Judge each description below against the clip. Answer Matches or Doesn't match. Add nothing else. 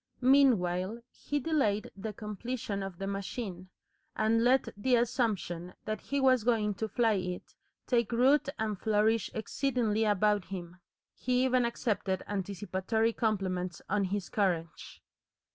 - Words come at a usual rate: Doesn't match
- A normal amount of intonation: Matches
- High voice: Matches